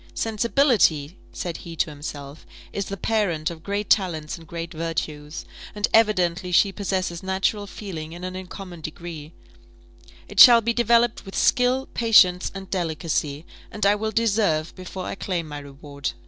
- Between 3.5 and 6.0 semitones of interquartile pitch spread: Yes, average, 4.6 semitones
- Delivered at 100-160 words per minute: Yes, average, 155 wpm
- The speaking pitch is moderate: Yes, medium, 180 Hz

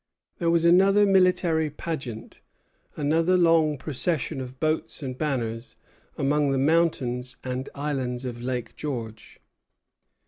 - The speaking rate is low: Yes, slow, 115 wpm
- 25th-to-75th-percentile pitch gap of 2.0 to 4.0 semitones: No, average, 4.6 semitones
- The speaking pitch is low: No, medium, 145 Hz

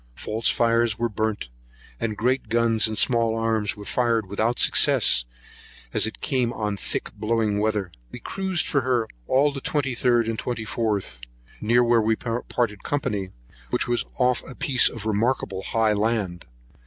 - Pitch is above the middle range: No, low, 115 Hz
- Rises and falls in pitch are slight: Yes, narrow, 2.2 semitones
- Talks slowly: No, average, 155 wpm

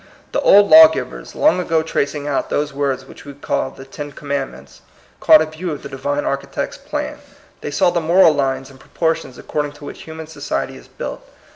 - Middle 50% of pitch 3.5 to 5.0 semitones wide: No, average, 2.7 semitones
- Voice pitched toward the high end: No, medium, 145 Hz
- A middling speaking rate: No, fast, 210 wpm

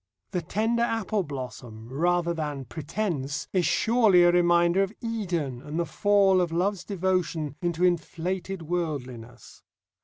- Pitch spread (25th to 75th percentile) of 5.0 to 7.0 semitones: No, average, 4.3 semitones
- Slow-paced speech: Yes, slow, 130 wpm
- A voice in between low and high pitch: Yes, medium, 175 Hz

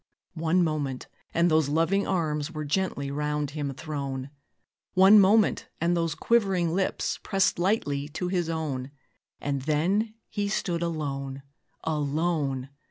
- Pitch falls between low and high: Yes, medium, 160 Hz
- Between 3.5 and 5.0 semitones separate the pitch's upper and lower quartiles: Yes, average, 4.1 semitones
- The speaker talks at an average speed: No, slow, 130 wpm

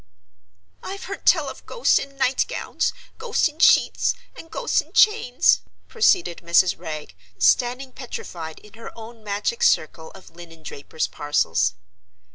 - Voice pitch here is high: Yes, high, 230 Hz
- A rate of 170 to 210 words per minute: No, average, 140 wpm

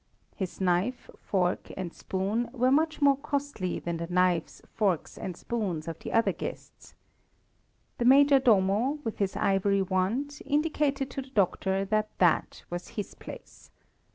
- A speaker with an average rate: Yes, average, 150 wpm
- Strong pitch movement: Yes, wide, 6.2 semitones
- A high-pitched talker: Yes, high, 205 Hz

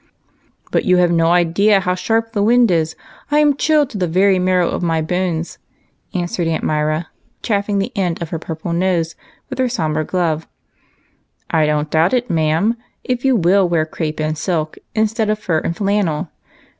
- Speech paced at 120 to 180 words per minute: No, average, 190 wpm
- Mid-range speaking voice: Yes, medium, 180 Hz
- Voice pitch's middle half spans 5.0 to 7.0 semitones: No, average, 4.2 semitones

